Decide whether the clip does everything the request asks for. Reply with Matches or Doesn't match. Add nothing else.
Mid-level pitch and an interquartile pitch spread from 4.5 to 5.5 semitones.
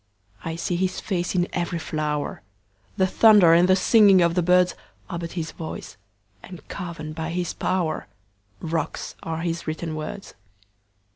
Doesn't match